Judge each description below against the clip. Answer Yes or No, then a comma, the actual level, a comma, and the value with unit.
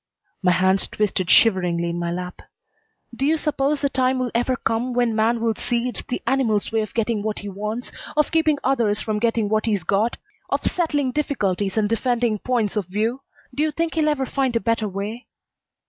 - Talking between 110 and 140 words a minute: No, average, 200 wpm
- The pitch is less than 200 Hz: No, high, 230 Hz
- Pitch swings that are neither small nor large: Yes, average, 4.0 semitones